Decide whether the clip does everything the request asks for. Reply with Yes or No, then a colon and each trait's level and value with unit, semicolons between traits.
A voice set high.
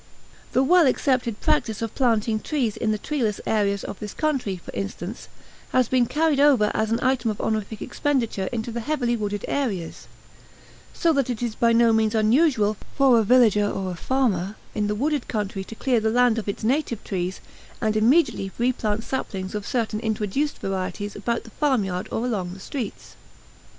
Yes: high, 225 Hz